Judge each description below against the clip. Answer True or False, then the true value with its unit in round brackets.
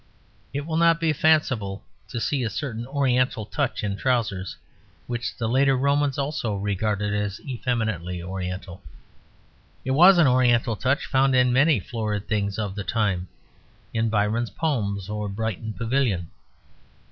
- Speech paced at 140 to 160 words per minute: True (145 wpm)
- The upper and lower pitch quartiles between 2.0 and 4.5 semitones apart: False (4.9 semitones)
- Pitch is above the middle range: False (115 Hz)